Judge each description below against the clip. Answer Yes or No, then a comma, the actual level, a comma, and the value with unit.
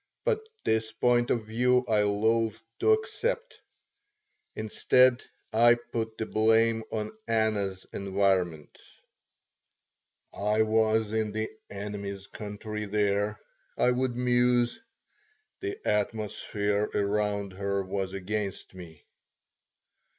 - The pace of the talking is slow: Yes, slow, 100 wpm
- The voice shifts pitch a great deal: No, average, 2.7 semitones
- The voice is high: No, low, 110 Hz